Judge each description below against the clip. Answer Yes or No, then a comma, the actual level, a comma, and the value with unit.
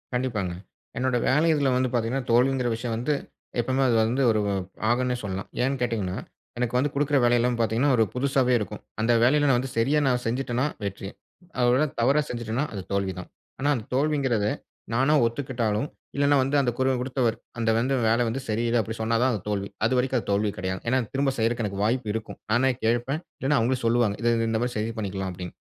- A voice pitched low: Yes, low, 120 Hz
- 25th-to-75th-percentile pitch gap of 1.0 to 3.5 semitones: Yes, average, 3.0 semitones